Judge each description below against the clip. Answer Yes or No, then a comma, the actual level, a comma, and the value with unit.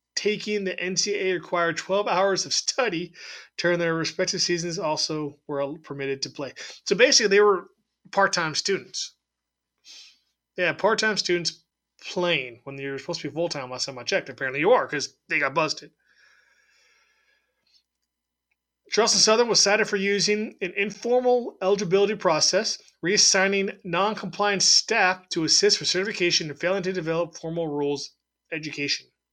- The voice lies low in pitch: No, medium, 180 Hz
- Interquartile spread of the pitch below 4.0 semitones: No, average, 4.5 semitones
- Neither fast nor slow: Yes, average, 145 wpm